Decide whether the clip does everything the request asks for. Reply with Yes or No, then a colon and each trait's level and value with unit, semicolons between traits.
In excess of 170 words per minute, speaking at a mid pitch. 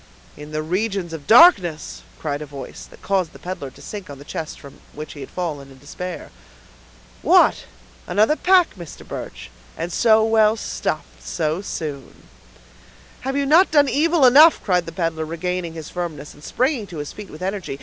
Yes: average, 180 wpm; medium, 175 Hz